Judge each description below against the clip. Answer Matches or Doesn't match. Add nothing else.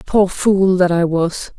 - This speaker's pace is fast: Doesn't match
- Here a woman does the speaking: Matches